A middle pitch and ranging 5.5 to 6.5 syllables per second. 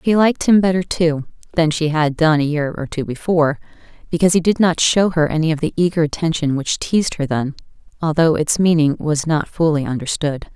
Yes: medium, 160 Hz; 5.7 syllables/s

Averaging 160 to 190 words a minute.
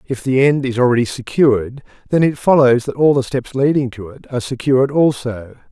No: average, 200 wpm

